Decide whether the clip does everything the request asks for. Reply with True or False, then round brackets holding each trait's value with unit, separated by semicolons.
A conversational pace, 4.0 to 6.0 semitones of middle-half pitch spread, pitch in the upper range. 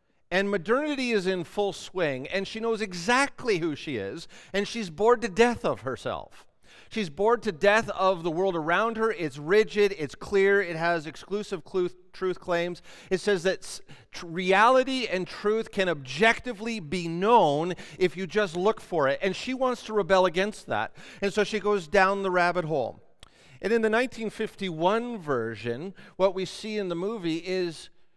False (180 wpm; 3.4 semitones; 195 Hz)